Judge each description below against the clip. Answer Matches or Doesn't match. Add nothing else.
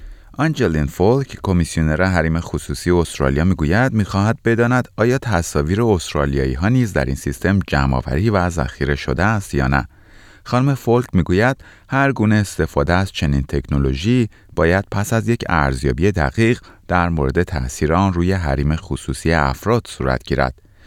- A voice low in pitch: Matches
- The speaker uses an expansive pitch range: Matches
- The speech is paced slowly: Doesn't match